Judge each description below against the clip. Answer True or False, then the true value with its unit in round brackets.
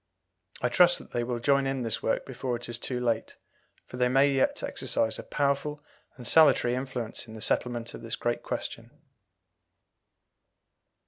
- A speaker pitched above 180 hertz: False (125 Hz)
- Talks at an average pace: True (170 wpm)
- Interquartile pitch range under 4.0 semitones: True (2.5 semitones)